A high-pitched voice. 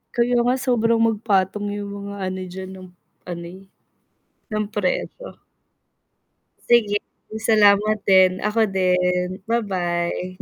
Yes: high, 200 Hz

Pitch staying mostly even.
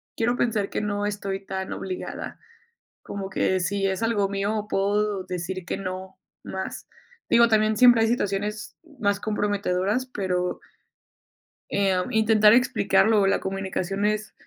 Yes: narrow, 1.9 semitones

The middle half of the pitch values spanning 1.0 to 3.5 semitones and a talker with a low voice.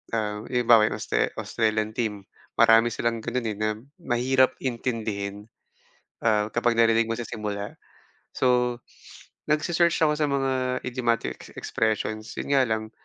Yes: average, 2.8 semitones; low, 115 Hz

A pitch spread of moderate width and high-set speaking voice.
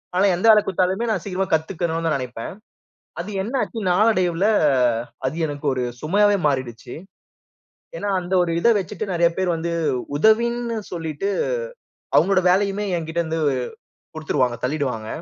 No: average, 4.5 semitones; medium, 175 Hz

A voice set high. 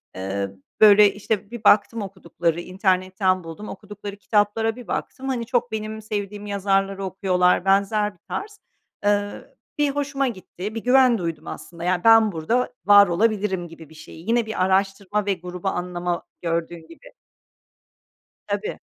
Yes: high, 200 Hz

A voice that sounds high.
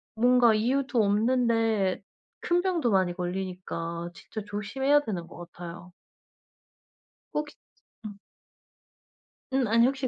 Yes: high, 220 Hz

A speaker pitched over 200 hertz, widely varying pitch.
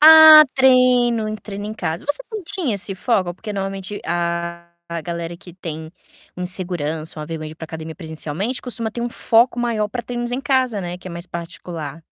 No: high, 190 Hz; wide, 6.0 semitones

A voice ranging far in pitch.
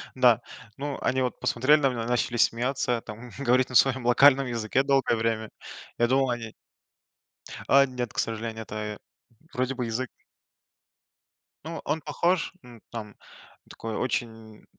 No: average, 2.7 semitones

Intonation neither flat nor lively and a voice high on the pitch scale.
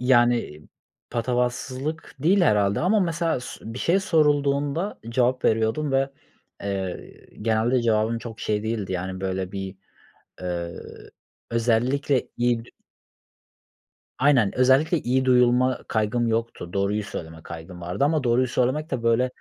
No: average, 4.2 semitones; low, 120 Hz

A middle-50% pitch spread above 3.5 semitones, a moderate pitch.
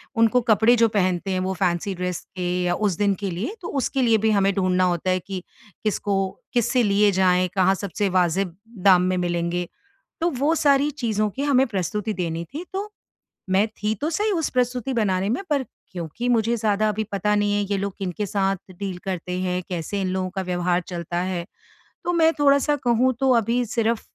No: average, 4.5 semitones; high, 200 Hz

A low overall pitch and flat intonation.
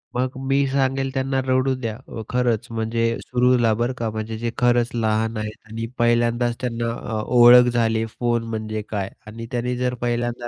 Yes: low, 120 Hz; narrow, 1.7 semitones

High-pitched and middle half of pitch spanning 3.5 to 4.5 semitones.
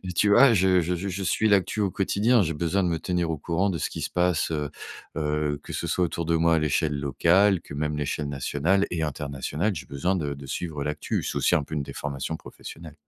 No: very low, 80 Hz; average, 3.8 semitones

